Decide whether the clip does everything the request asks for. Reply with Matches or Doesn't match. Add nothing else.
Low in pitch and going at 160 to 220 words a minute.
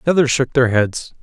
Doesn't match